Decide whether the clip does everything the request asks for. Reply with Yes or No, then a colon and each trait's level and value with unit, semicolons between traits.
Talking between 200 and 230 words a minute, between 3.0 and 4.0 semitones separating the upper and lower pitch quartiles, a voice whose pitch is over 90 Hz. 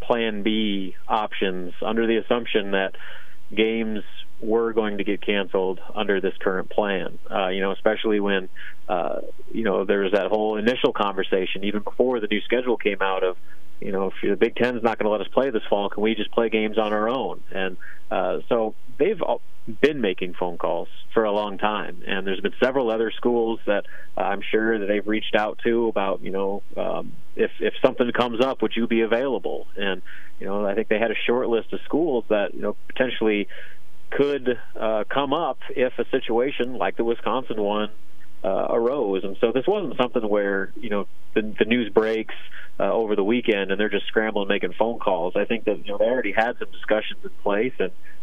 No: fast, 205 wpm; narrow, 2.5 semitones; low, 110 Hz